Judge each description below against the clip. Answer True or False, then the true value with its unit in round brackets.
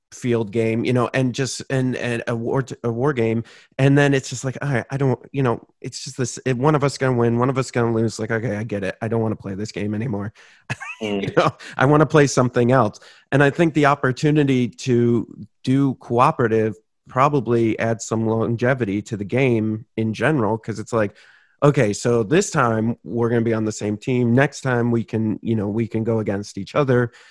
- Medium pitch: False (120 Hz)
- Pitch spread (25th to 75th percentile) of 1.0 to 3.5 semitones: True (3.1 semitones)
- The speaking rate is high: True (225 wpm)